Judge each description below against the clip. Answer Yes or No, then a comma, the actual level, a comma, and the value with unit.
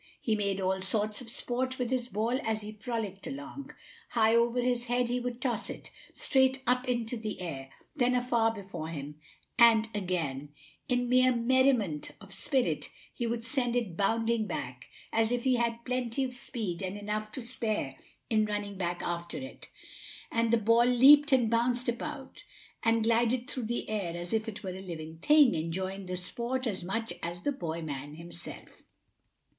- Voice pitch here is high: Yes, high, 225 Hz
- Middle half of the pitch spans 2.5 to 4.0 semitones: No, average, 4.5 semitones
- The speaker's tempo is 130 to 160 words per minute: No, average, 180 wpm